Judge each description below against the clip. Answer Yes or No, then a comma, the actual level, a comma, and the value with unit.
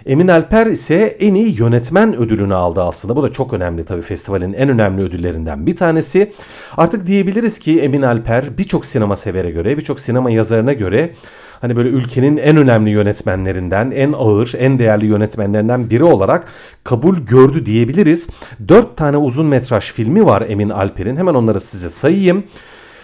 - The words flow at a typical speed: No, fast, 160 wpm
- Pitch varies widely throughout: Yes, wide, 6.7 semitones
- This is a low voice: Yes, low, 120 Hz